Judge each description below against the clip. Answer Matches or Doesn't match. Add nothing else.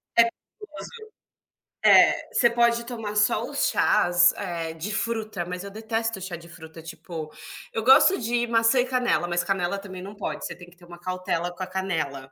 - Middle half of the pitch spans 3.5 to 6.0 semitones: Matches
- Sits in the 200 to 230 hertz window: Doesn't match